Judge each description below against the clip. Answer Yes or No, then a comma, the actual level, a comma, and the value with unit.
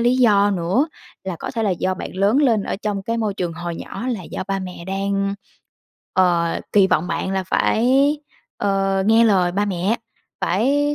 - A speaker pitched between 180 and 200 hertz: Yes, high, 195 Hz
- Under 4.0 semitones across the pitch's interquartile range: Yes, average, 3.0 semitones